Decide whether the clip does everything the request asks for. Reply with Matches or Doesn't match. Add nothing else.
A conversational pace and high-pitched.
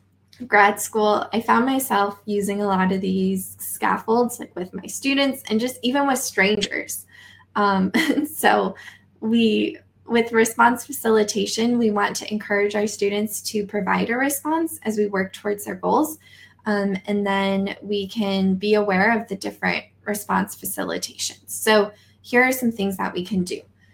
Matches